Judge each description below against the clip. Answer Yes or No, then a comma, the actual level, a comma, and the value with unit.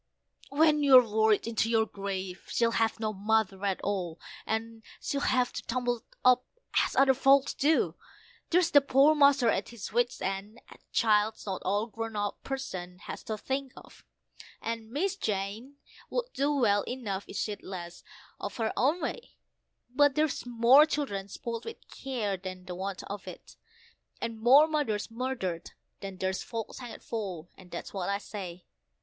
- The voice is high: Yes, high, 225 Hz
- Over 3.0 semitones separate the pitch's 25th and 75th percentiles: Yes, average, 5.0 semitones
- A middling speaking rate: Yes, average, 165 wpm